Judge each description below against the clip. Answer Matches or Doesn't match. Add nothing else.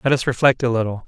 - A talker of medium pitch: Doesn't match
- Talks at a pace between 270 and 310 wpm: Matches